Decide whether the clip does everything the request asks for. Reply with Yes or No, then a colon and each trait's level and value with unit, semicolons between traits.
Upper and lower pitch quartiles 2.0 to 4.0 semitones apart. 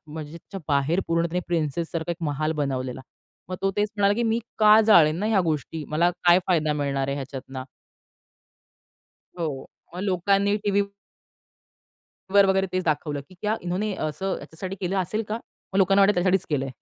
No: average, 4.5 semitones